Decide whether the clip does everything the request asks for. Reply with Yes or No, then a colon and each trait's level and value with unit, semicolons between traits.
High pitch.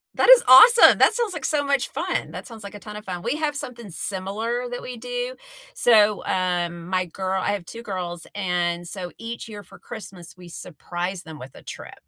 Yes: high, 200 Hz